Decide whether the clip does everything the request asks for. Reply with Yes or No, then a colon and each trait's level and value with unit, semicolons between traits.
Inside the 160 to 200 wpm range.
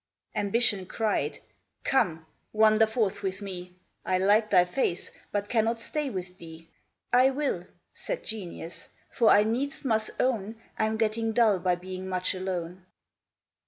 No: average, 140 wpm